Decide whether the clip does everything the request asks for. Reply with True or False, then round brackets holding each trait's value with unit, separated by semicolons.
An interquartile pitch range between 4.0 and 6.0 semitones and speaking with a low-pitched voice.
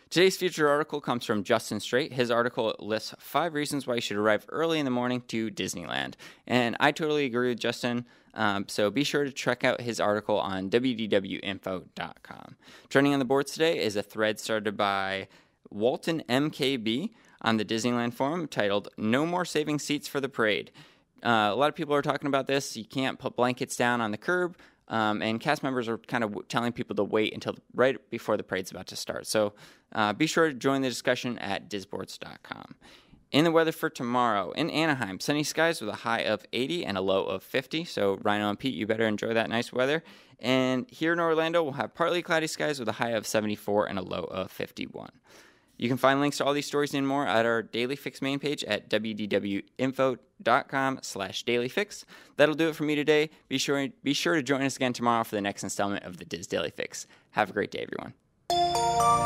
True (4.8 semitones; 130 Hz)